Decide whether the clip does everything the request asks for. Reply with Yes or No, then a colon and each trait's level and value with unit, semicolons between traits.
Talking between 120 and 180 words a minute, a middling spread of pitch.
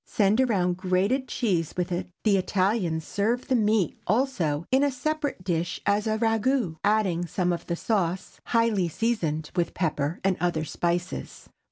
Yes: average, 160 wpm; average, 4.6 semitones